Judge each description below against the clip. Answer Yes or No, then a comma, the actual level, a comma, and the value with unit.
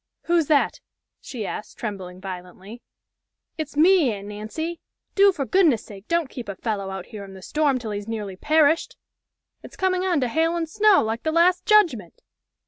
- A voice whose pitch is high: Yes, very high, 260 Hz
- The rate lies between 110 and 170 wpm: No, average, 180 wpm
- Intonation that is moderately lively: No, wide, 8.5 semitones